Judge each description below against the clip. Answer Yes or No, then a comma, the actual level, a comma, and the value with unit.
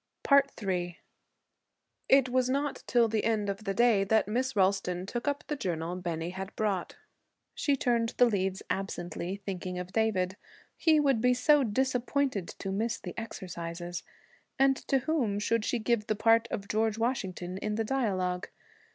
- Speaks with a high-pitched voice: Yes, high, 215 Hz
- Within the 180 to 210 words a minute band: No, average, 160 wpm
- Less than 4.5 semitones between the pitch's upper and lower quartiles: No, average, 4.8 semitones